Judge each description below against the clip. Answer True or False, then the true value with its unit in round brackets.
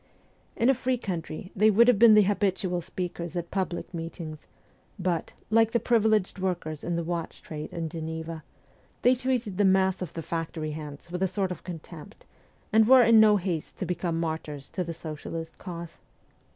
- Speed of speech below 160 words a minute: False (180 wpm)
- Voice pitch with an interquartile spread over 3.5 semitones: True (4.2 semitones)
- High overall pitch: False (180 Hz)